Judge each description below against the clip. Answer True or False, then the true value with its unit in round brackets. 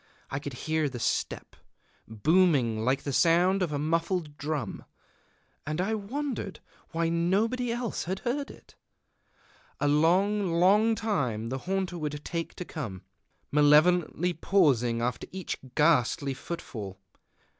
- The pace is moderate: False (125 wpm)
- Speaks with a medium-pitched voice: True (165 Hz)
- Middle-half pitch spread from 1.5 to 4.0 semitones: False (5.1 semitones)